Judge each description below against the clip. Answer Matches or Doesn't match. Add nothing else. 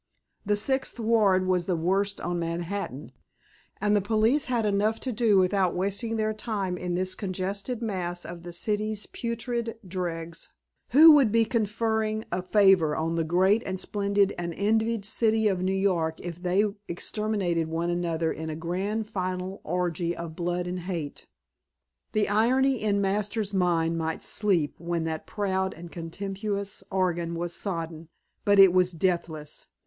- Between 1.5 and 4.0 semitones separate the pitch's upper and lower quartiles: Matches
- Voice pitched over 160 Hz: Matches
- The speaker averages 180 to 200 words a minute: Doesn't match